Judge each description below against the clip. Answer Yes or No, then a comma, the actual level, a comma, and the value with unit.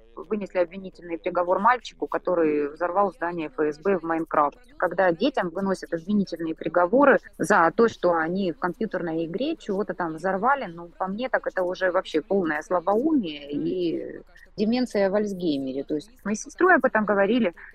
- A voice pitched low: No, medium, 185 Hz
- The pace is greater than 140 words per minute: Yes, average, 155 wpm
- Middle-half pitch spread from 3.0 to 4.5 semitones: Yes, average, 4.0 semitones